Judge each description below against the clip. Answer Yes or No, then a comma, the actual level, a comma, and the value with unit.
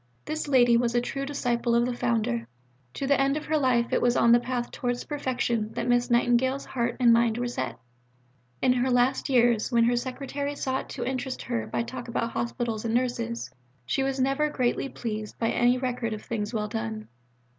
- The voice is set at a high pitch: Yes, high, 245 Hz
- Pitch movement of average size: No, narrow, 1.9 semitones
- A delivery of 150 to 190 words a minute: No, fast, 205 wpm